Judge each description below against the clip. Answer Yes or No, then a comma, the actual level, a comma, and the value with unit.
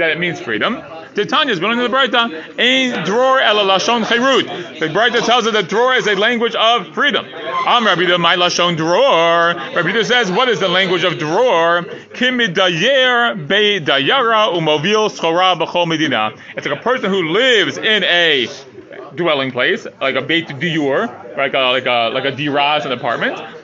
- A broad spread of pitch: Yes, wide, 6.4 semitones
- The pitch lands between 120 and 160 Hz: No, medium, 180 Hz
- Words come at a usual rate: Yes, average, 160 wpm